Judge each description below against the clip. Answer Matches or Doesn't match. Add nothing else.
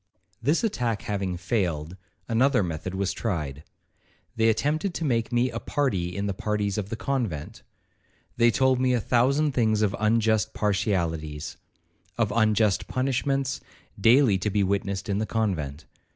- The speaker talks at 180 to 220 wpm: Doesn't match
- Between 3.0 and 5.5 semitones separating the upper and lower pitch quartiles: Matches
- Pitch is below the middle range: Matches